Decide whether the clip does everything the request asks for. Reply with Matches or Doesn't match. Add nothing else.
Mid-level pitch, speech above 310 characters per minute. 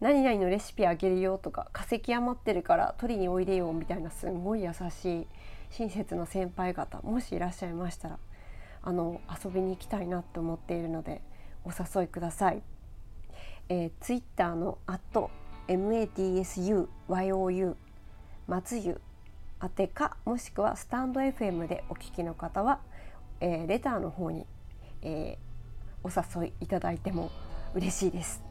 Doesn't match